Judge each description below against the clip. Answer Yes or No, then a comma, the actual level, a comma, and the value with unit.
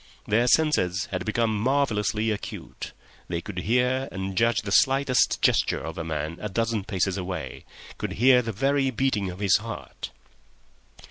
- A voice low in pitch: Yes, low, 110 Hz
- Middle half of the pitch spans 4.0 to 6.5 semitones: Yes, average, 4.8 semitones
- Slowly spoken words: No, average, 150 wpm